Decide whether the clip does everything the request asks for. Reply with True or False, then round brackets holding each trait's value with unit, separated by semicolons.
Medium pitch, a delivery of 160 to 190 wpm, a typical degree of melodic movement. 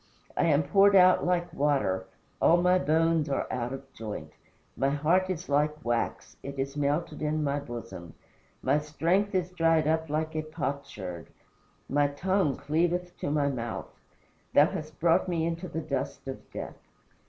True (150 Hz; 165 wpm; 3.4 semitones)